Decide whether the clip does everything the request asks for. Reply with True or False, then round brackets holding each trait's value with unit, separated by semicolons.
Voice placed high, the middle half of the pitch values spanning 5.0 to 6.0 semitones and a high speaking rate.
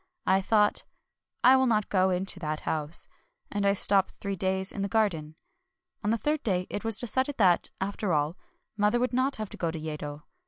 False (200 Hz; 3.8 semitones; 210 wpm)